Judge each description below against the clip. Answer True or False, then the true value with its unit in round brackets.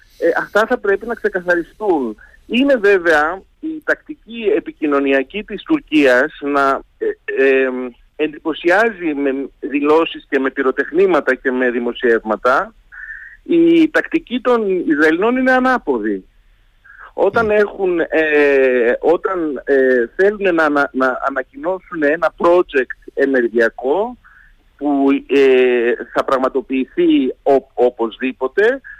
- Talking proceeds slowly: True (105 wpm)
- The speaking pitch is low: False (155 Hz)